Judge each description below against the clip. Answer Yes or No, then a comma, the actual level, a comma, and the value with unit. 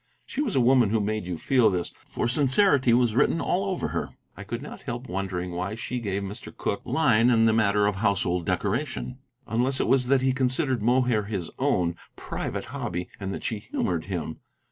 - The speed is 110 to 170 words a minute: No, average, 200 wpm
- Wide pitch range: No, average, 4.9 semitones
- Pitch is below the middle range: Yes, low, 110 Hz